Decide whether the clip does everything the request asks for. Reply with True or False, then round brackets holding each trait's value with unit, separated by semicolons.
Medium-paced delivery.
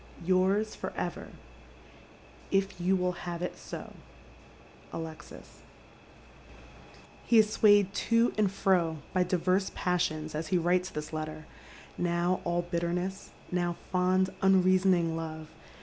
False (125 wpm)